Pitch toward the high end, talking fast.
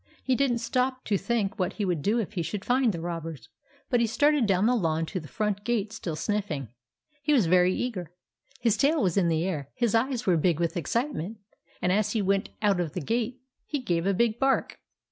Yes: high, 205 Hz; fast, 225 wpm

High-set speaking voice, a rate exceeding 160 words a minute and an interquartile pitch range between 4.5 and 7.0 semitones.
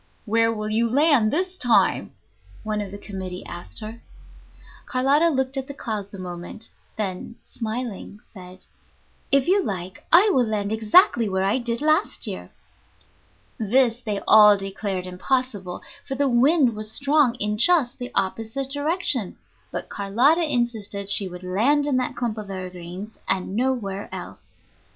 No: high, 225 Hz; average, 150 wpm; average, 5.0 semitones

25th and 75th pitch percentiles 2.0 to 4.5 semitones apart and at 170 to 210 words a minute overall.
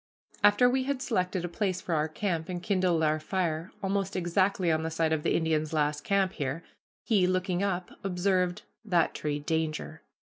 Yes: average, 3.3 semitones; average, 180 wpm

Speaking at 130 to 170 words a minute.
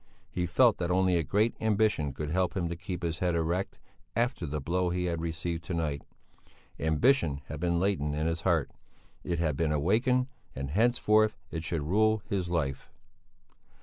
No: average, 180 wpm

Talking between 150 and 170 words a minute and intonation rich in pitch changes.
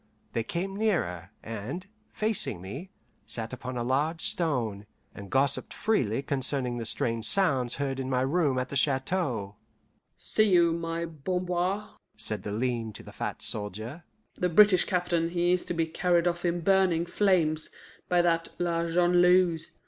Yes: average, 155 wpm; wide, 5.9 semitones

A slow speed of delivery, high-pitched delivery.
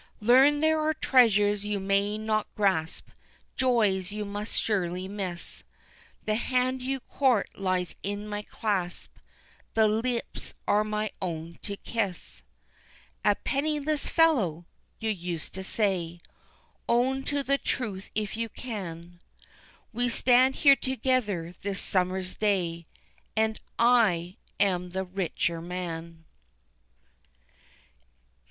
Yes: slow, 115 wpm; high, 205 Hz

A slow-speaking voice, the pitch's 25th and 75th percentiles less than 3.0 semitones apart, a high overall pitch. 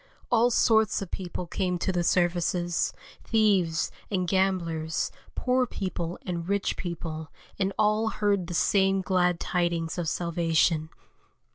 No: slow, 130 wpm; narrow, 2.6 semitones; medium, 180 Hz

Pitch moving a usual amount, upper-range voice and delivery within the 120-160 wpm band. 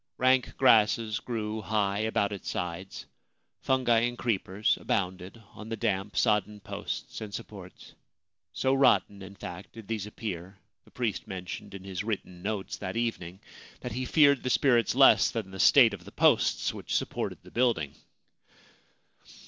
No: average, 3.3 semitones; low, 105 Hz; average, 155 wpm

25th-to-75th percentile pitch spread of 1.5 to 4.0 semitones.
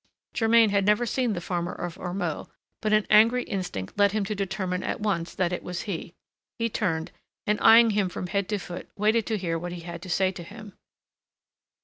Yes: average, 3.2 semitones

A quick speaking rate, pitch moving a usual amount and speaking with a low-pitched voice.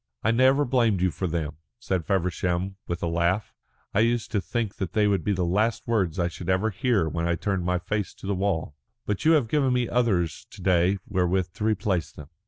Yes: fast, 215 wpm; average, 4.1 semitones; very low, 95 Hz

